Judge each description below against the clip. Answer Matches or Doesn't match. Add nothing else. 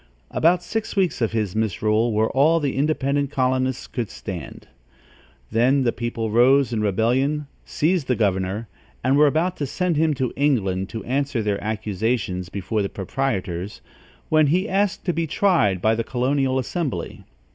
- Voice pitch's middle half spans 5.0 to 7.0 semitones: Matches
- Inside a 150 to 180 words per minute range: Matches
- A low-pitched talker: Matches